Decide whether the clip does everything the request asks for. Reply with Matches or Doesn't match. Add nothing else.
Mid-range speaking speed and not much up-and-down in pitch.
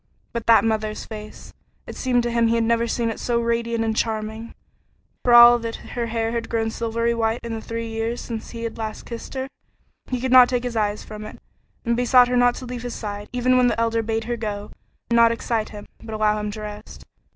Doesn't match